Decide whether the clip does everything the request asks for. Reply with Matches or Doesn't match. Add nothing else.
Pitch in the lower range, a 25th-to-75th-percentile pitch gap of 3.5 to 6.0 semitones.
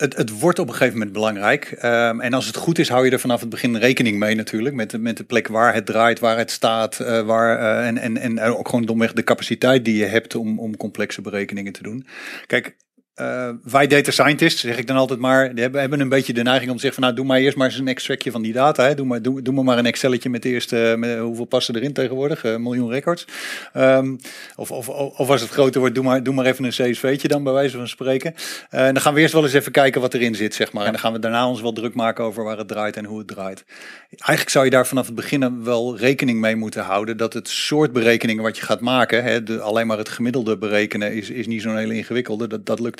Doesn't match